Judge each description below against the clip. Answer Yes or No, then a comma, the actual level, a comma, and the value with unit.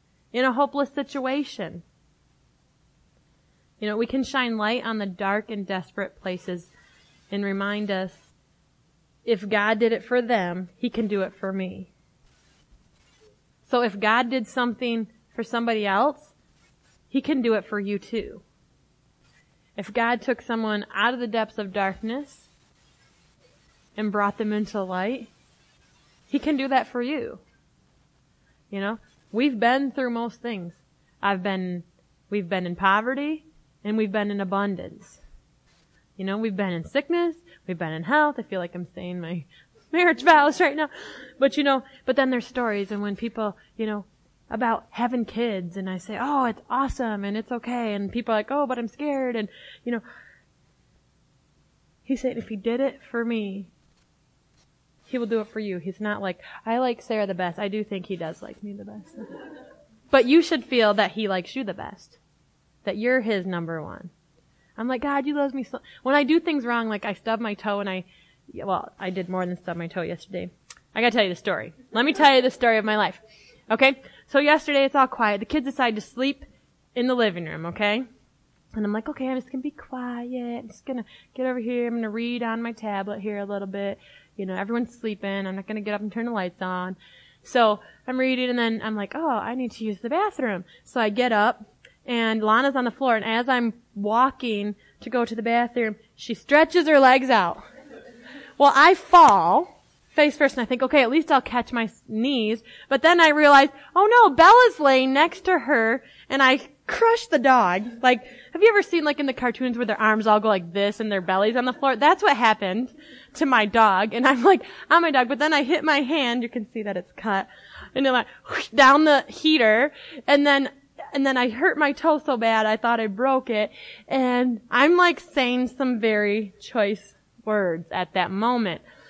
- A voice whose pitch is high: Yes, high, 230 Hz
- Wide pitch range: No, average, 4.6 semitones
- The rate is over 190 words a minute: Yes, average, 200 wpm